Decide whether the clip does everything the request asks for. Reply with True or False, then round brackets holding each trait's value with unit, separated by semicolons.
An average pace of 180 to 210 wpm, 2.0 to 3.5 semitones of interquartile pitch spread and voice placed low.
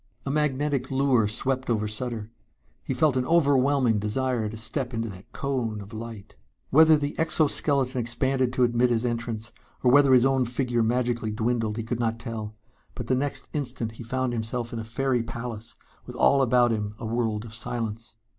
True (185 wpm; 2.7 semitones; 120 Hz)